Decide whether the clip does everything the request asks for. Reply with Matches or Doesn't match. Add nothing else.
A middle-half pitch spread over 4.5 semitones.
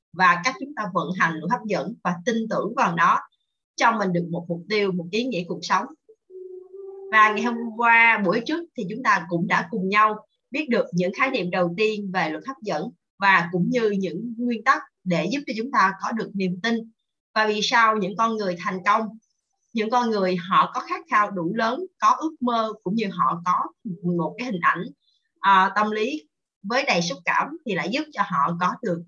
Matches